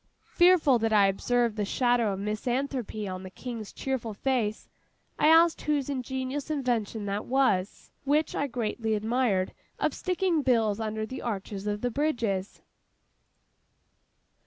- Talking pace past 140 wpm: No, slow, 135 wpm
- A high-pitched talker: Yes, high, 235 Hz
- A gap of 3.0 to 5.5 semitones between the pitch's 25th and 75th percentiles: Yes, average, 4.4 semitones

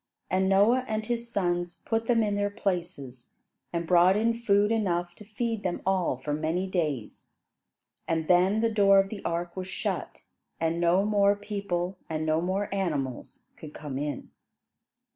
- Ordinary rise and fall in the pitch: Yes, average, 3.4 semitones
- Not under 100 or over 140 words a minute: No, average, 165 wpm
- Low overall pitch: No, medium, 185 Hz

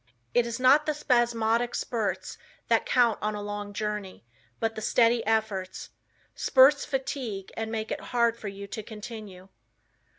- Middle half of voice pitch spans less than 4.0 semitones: Yes, average, 2.7 semitones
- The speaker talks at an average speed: Yes, average, 155 wpm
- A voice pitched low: No, high, 225 Hz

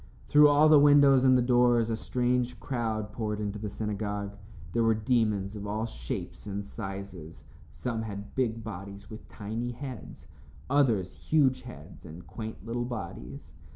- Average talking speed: Yes, average, 155 wpm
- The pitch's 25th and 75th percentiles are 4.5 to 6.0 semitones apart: No, average, 3.5 semitones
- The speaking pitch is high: No, low, 110 Hz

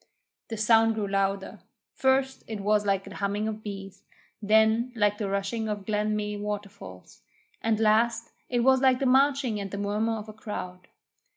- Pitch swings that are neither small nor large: No, narrow, 2.1 semitones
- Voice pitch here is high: Yes, high, 215 Hz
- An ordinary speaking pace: Yes, average, 175 wpm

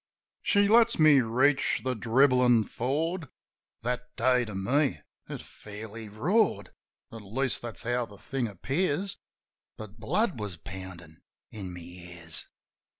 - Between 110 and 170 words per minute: Yes, slow, 135 wpm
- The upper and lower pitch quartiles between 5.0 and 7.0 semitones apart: Yes, average, 5.3 semitones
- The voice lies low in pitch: Yes, low, 120 Hz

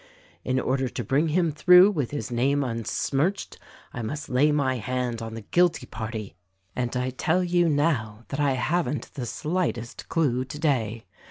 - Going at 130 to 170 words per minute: Yes, average, 165 wpm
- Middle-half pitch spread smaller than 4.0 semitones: No, average, 4.6 semitones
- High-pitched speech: No, low, 135 Hz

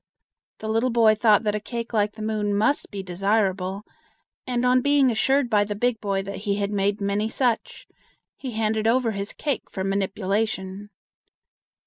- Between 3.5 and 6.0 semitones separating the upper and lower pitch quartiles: No, average, 2.7 semitones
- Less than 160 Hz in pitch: No, high, 215 Hz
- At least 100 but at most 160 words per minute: No, average, 170 wpm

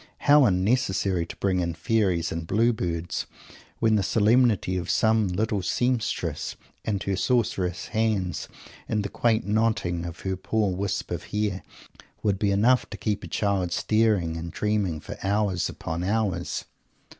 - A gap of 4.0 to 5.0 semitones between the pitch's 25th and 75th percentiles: No, average, 3.4 semitones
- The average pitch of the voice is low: Yes, low, 100 Hz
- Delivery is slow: No, average, 155 wpm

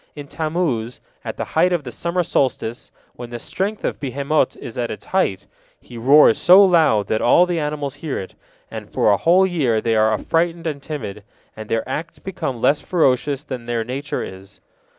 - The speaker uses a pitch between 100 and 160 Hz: Yes, medium, 140 Hz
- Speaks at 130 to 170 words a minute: No, average, 190 wpm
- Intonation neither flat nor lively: No, wide, 6.2 semitones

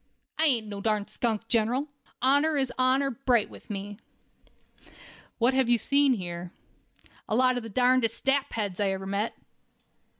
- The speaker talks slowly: No, average, 160 wpm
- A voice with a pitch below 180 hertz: No, high, 235 Hz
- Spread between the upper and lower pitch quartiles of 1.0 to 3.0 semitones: No, average, 4.2 semitones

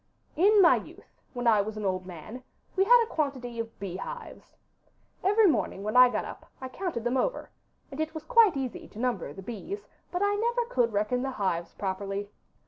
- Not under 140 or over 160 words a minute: No, average, 200 wpm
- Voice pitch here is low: No, very high, 250 Hz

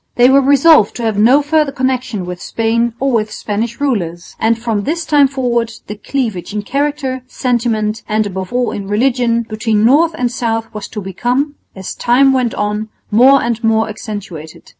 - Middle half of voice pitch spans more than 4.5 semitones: No, average, 3.7 semitones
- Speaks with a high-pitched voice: Yes, high, 235 Hz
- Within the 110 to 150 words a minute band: No, average, 180 wpm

